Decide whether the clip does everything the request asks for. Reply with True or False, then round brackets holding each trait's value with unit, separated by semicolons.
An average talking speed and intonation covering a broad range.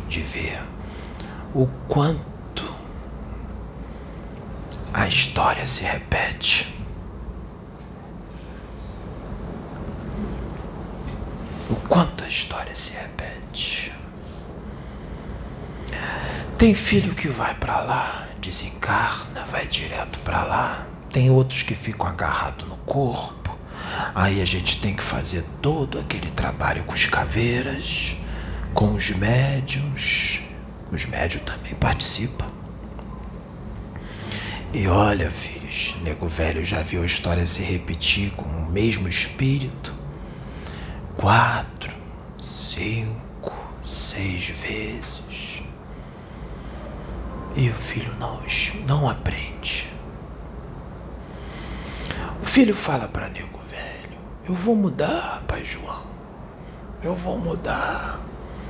False (90 wpm; 6.9 semitones)